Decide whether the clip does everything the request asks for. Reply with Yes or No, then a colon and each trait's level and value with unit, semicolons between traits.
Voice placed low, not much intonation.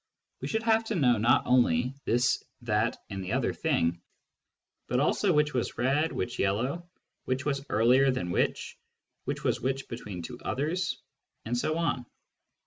No: low, 125 Hz; average, 4.3 semitones